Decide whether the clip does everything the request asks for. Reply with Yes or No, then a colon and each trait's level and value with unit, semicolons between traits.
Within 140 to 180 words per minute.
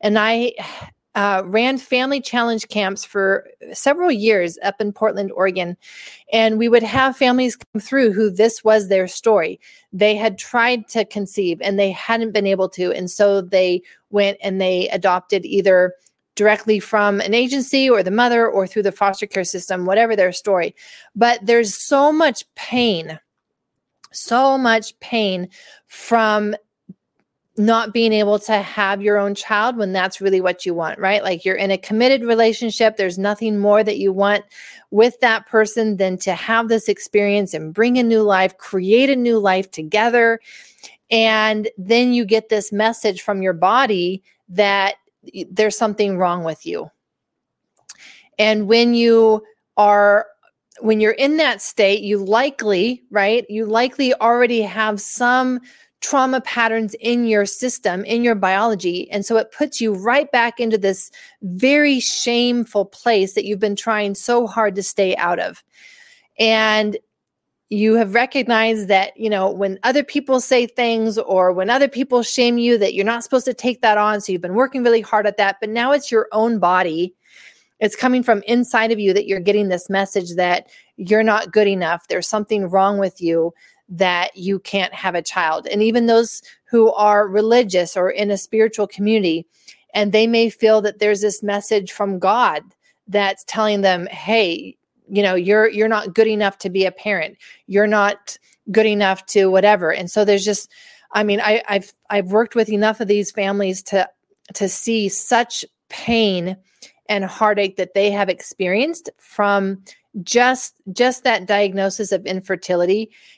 Yes: average, 170 wpm